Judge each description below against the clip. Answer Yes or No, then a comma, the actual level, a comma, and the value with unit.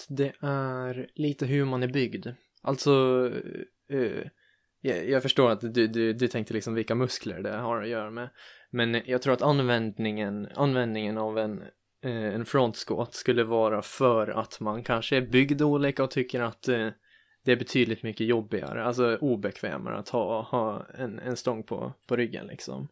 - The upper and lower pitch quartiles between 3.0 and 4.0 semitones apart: No, narrow, 2.5 semitones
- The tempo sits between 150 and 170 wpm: Yes, average, 160 wpm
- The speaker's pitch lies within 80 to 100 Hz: No, low, 120 Hz